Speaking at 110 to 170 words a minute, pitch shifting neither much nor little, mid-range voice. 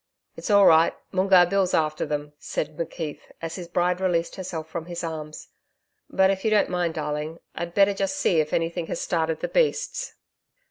No: average, 185 wpm; average, 3.0 semitones; medium, 170 Hz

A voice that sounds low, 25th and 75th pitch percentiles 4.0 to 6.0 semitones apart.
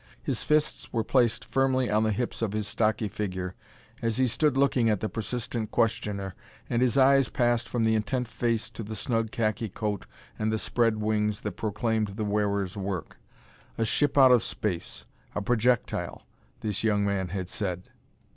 No: low, 110 Hz; average, 2.7 semitones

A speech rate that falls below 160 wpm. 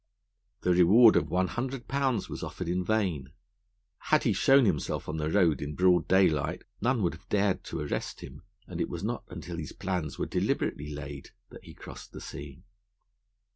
No: average, 185 wpm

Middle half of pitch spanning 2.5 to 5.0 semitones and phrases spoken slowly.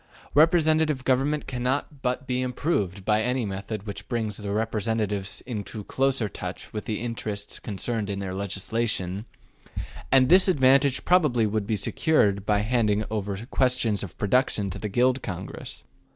No: average, 4.1 semitones; average, 150 wpm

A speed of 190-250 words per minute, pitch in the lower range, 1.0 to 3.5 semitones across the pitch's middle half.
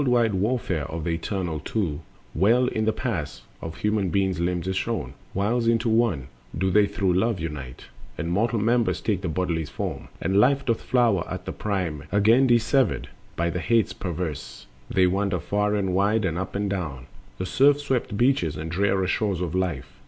No: average, 195 wpm; very low, 95 Hz; average, 4.5 semitones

